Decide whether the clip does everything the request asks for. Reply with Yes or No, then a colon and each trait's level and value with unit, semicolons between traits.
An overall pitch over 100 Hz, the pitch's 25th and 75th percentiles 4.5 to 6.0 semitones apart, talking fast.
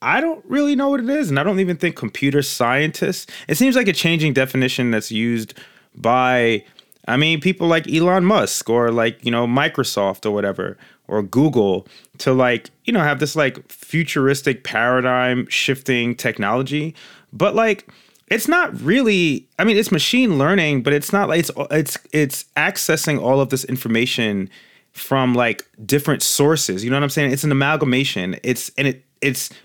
No: medium, 140 Hz; wide, 5.4 semitones; average, 175 wpm